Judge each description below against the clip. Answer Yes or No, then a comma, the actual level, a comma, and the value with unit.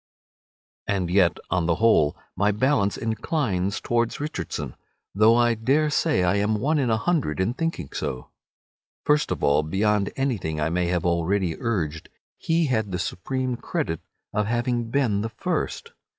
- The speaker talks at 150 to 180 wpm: Yes, average, 160 wpm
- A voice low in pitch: Yes, low, 105 Hz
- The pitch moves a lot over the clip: Yes, wide, 6.0 semitones